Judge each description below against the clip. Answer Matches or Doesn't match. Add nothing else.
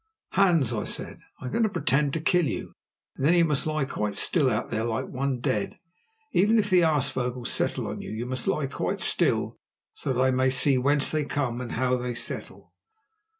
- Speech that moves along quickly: Matches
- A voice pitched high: Doesn't match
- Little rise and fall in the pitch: Doesn't match